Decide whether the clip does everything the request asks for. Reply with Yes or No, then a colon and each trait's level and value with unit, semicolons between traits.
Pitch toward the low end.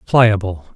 Yes: low, 100 Hz